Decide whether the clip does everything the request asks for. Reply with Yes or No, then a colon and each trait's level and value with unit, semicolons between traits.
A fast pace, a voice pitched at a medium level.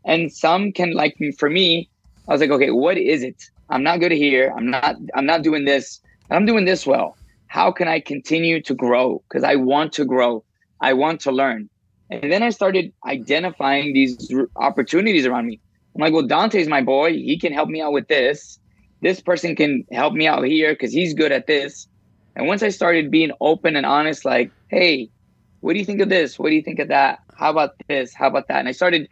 Yes: fast, 225 wpm; medium, 155 Hz